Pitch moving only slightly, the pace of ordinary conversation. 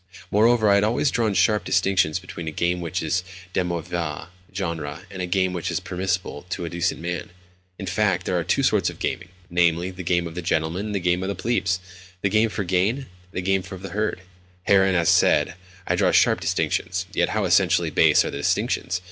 No: narrow, 1.9 semitones; fast, 210 wpm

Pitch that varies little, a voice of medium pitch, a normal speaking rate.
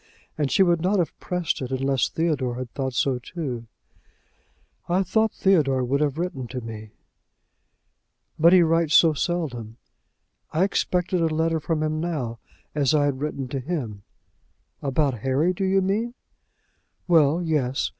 No: average, 4.8 semitones; medium, 150 Hz; average, 155 wpm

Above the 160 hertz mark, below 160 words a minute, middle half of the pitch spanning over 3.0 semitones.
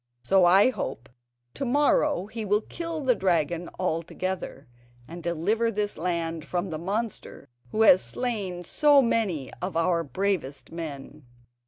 Yes: medium, 185 Hz; average, 140 wpm; average, 5.0 semitones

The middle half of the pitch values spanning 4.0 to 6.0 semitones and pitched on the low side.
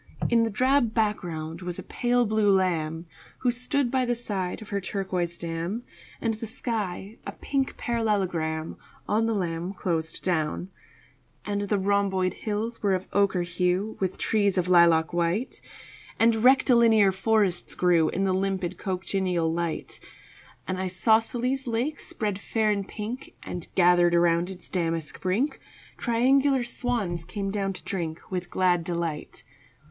No: average, 4.4 semitones; high, 195 Hz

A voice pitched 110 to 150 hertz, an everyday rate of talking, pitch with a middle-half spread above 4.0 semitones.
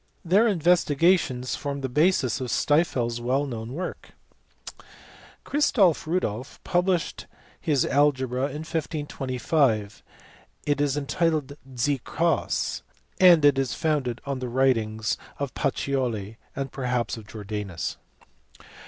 No: medium, 140 Hz; slow, 110 wpm; average, 4.4 semitones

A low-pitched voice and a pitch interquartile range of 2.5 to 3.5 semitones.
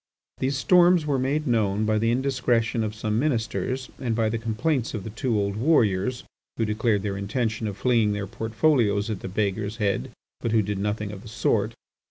Yes: low, 110 Hz; average, 3.2 semitones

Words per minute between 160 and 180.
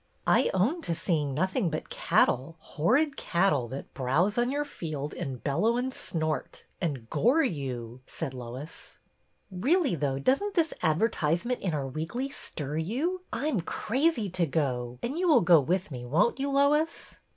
Yes: average, 170 wpm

